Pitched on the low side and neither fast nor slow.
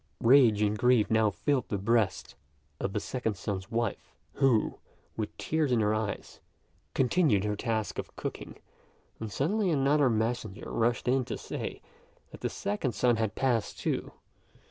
Yes: low, 115 Hz; average, 155 wpm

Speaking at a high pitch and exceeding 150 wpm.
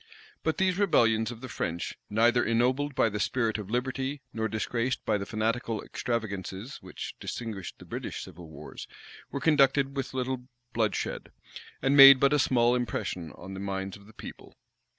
No: low, 120 Hz; average, 170 wpm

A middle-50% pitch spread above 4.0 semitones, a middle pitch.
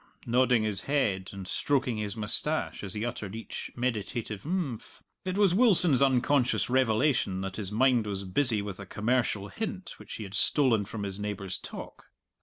No: average, 4.7 semitones; low, 115 Hz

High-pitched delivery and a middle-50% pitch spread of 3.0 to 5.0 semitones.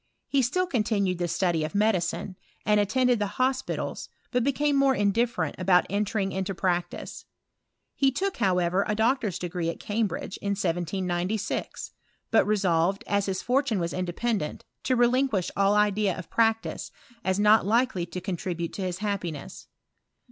Yes: high, 200 Hz; average, 4.1 semitones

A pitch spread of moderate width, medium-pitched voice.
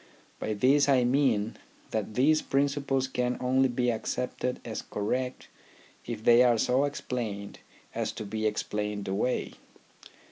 No: average, 3.4 semitones; low, 125 Hz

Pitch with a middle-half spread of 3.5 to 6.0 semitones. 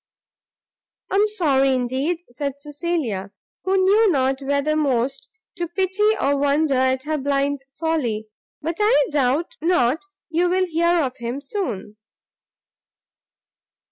Yes: average, 4.7 semitones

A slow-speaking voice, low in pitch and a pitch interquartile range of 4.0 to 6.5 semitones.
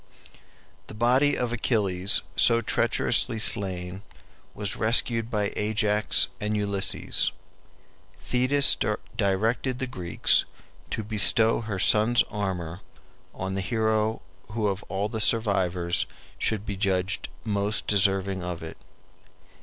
No: slow, 115 wpm; low, 105 Hz; average, 2.7 semitones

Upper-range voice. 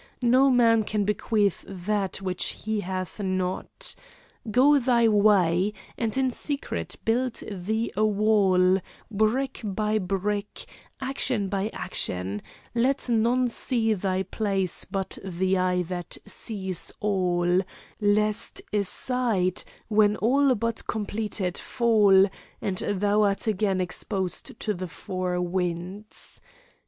Yes: high, 205 Hz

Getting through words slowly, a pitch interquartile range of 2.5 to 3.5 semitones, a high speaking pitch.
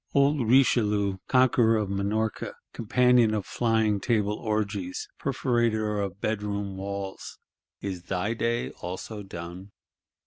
No: slow, 110 wpm; average, 2.8 semitones; low, 105 Hz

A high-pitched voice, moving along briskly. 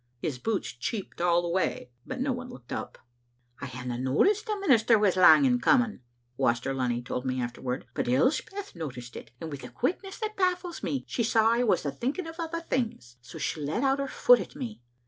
Yes: high, 210 Hz; fast, 215 wpm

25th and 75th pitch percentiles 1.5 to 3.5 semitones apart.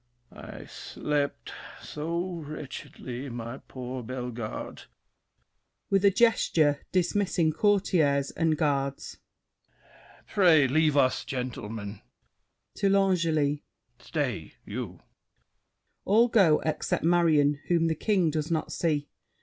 No: average, 4.1 semitones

